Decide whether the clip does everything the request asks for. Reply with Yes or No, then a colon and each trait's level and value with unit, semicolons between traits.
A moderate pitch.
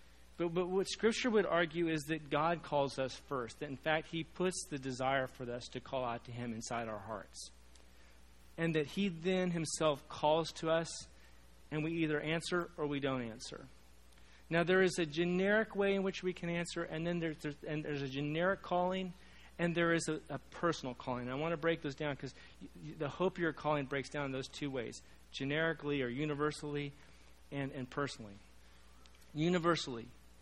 Yes: medium, 150 Hz